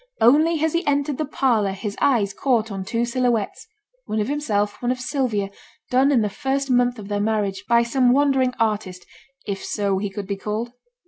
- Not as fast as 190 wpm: No, average, 195 wpm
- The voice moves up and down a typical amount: Yes, average, 4.5 semitones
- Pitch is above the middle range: Yes, high, 235 Hz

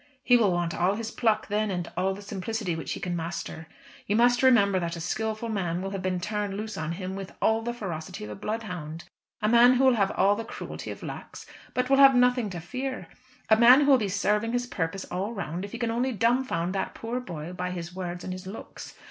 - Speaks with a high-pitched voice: Yes, high, 205 Hz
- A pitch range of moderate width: Yes, average, 4.5 semitones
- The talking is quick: Yes, fast, 240 wpm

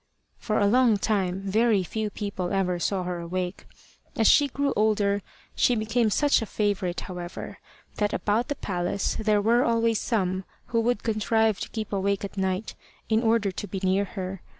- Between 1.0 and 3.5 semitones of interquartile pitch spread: Yes, average, 2.9 semitones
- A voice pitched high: Yes, high, 205 Hz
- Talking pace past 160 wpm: Yes, average, 175 wpm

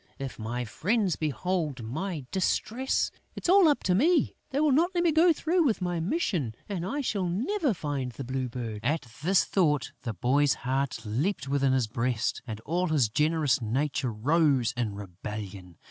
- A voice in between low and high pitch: Yes, medium, 145 Hz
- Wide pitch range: Yes, wide, 8.1 semitones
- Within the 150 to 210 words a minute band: Yes, average, 180 wpm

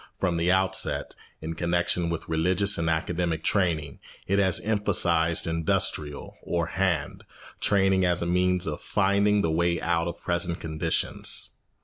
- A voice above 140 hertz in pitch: No, very low, 85 Hz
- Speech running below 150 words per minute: Yes, average, 140 wpm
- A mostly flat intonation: Yes, narrow, 2.3 semitones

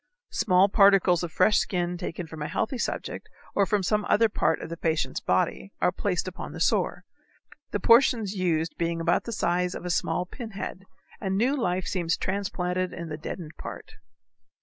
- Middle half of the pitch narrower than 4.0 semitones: Yes, average, 2.9 semitones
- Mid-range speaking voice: Yes, medium, 180 Hz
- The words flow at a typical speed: Yes, average, 180 wpm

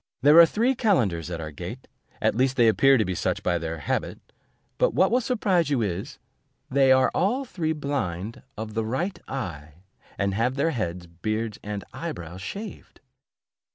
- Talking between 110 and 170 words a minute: No, average, 180 wpm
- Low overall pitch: Yes, low, 115 Hz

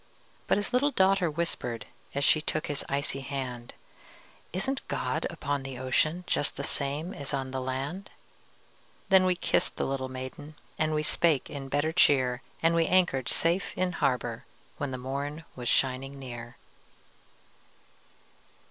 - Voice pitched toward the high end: No, medium, 140 Hz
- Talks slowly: No, average, 150 wpm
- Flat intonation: No, average, 4.3 semitones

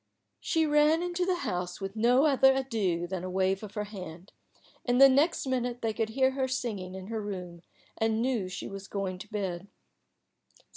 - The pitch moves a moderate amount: No, wide, 5.7 semitones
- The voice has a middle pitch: No, high, 220 Hz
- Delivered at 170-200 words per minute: Yes, average, 190 wpm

